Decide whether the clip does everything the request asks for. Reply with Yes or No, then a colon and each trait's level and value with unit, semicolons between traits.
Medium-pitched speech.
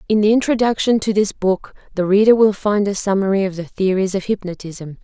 No: high, 200 Hz